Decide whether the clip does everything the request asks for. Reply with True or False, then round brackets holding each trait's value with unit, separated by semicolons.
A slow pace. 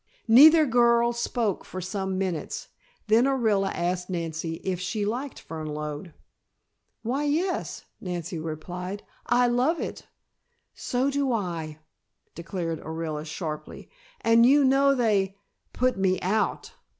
True (120 wpm)